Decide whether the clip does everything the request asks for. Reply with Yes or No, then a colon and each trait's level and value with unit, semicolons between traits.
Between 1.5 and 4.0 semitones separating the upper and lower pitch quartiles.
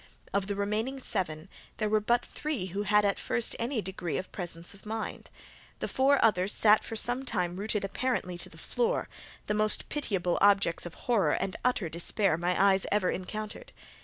Yes: average, 3.6 semitones